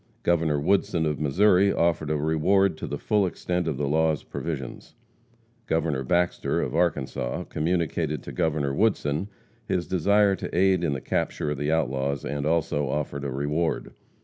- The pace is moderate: Yes, average, 160 wpm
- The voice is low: Yes, very low, 80 Hz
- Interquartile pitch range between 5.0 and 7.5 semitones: No, average, 3.3 semitones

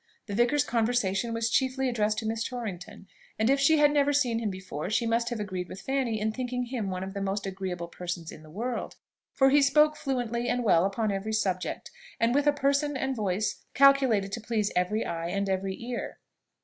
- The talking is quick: Yes, fast, 210 wpm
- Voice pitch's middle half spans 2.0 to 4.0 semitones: No, average, 4.8 semitones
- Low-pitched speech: No, high, 225 Hz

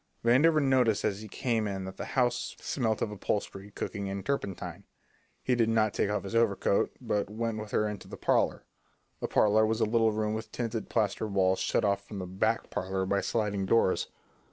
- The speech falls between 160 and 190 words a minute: No, average, 200 wpm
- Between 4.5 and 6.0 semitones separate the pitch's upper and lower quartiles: No, narrow, 2.4 semitones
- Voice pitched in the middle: No, low, 105 Hz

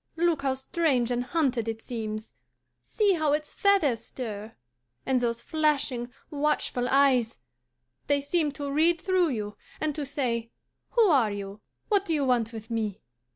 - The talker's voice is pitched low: No, very high, 265 Hz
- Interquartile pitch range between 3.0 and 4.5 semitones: No, average, 4.9 semitones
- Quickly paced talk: No, average, 155 wpm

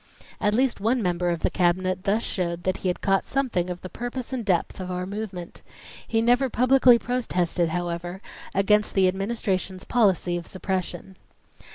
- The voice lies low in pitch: No, high, 190 Hz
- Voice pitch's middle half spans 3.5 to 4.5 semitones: Yes, average, 4.2 semitones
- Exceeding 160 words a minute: Yes, average, 170 wpm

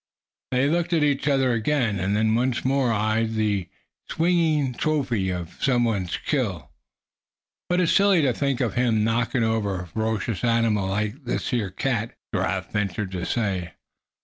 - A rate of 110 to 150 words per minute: No, average, 160 wpm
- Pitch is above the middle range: No, low, 115 Hz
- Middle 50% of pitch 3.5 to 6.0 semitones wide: Yes, average, 4.6 semitones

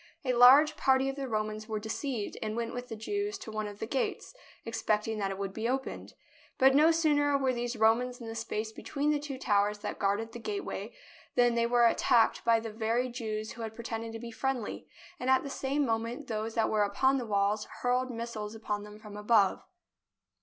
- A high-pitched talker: Yes, high, 230 Hz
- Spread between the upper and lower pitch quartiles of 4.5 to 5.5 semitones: No, average, 3.3 semitones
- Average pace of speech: No, fast, 215 wpm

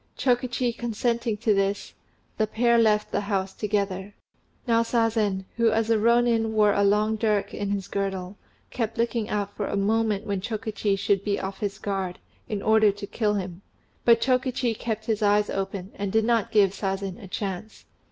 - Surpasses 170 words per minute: Yes, average, 180 wpm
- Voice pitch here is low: No, high, 210 Hz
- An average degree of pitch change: No, narrow, 2.3 semitones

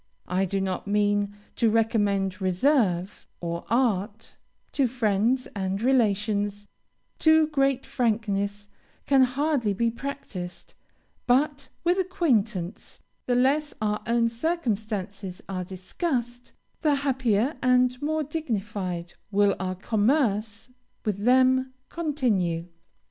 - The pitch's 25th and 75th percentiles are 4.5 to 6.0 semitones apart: Yes, average, 4.8 semitones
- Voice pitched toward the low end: No, high, 225 Hz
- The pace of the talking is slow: Yes, slow, 110 wpm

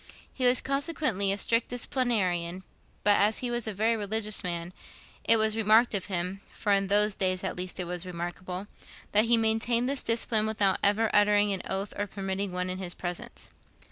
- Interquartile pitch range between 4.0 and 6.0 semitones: No, average, 3.3 semitones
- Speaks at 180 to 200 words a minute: Yes, average, 190 wpm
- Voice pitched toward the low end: No, high, 205 Hz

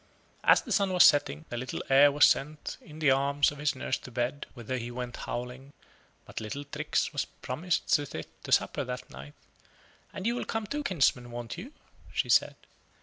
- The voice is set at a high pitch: No, medium, 140 Hz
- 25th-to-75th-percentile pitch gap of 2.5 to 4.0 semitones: Yes, average, 3.5 semitones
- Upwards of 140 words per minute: Yes, average, 200 wpm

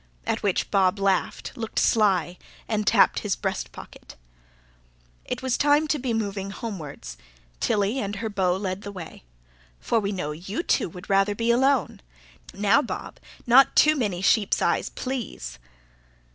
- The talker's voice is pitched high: Yes, high, 205 Hz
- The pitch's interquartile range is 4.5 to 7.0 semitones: No, average, 3.7 semitones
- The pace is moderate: Yes, average, 155 wpm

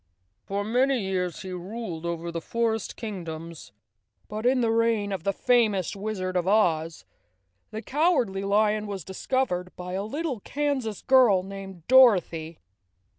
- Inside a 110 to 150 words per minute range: Yes, average, 140 wpm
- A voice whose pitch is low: No, high, 200 Hz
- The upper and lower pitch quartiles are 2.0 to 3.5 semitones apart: No, average, 4.3 semitones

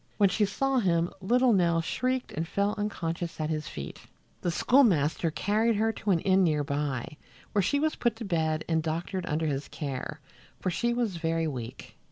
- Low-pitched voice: No, medium, 175 Hz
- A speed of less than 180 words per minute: No, average, 190 wpm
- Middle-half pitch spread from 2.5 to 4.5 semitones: No, average, 5.1 semitones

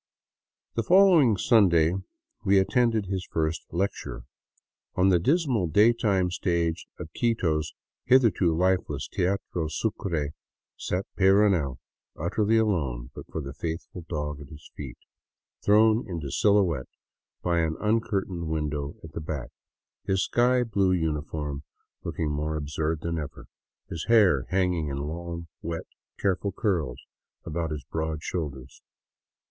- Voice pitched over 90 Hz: No, very low, 85 Hz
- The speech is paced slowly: Yes, slow, 130 wpm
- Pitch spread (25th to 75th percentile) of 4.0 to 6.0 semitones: Yes, average, 4.6 semitones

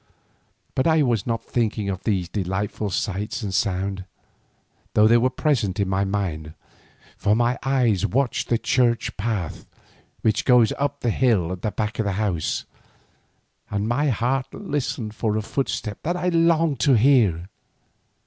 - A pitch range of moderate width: Yes, average, 4.5 semitones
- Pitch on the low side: Yes, low, 110 Hz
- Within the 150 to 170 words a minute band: Yes, average, 160 wpm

